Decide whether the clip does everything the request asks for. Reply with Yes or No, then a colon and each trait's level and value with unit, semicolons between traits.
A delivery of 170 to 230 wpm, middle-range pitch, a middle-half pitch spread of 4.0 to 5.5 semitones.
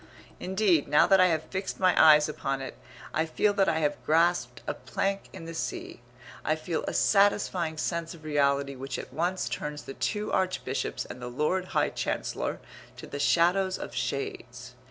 Yes: average, 180 wpm; medium, 160 Hz; average, 4.7 semitones